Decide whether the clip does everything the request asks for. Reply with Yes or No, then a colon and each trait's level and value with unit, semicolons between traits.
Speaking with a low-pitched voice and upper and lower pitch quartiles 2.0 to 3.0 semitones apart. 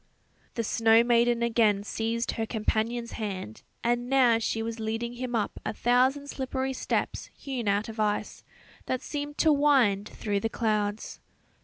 No: high, 230 Hz; narrow, 2.4 semitones